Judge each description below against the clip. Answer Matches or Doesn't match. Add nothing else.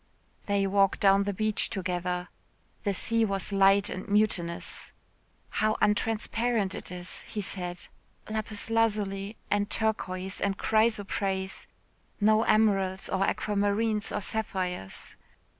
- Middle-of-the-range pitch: Doesn't match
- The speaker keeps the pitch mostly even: Matches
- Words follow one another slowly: Matches